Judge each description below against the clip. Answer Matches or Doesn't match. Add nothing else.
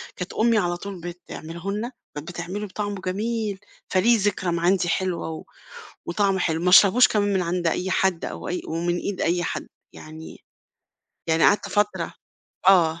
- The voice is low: Doesn't match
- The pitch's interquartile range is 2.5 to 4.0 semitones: Matches